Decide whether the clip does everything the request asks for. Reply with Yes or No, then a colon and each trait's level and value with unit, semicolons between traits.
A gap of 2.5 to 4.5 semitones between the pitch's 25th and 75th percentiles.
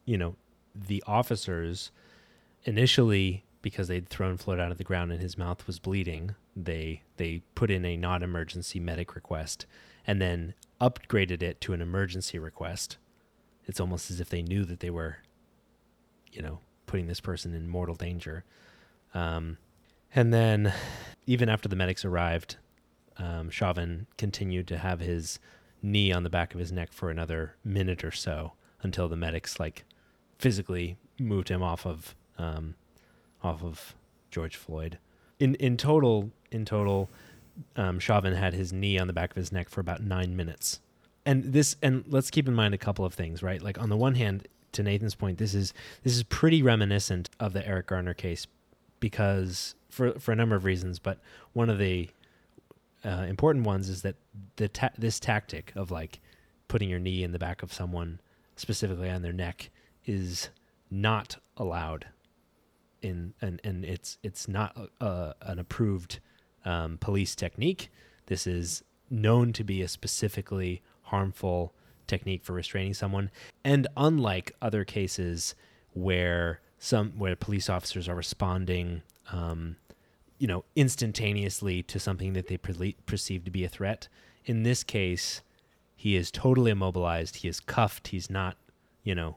Yes: average, 3.2 semitones